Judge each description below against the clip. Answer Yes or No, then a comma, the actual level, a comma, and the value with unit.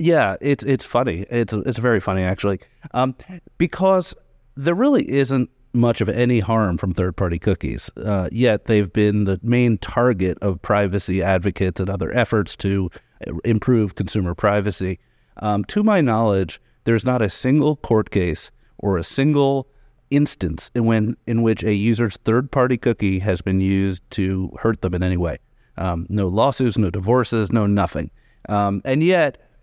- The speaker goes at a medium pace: Yes, average, 160 wpm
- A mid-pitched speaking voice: No, low, 110 Hz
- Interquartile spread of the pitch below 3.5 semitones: No, average, 4.7 semitones